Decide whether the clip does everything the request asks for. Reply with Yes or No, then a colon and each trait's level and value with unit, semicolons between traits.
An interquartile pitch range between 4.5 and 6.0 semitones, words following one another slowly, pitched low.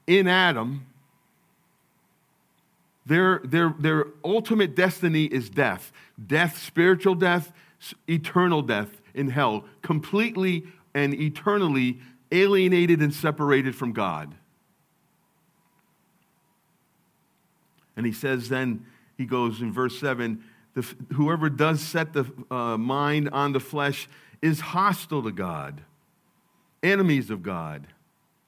No: wide, 5.4 semitones; slow, 105 wpm; medium, 155 Hz